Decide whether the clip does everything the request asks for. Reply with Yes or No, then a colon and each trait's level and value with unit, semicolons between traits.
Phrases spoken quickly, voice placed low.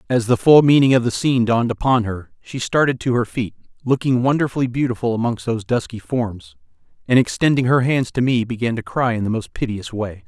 Yes: fast, 210 wpm; low, 120 Hz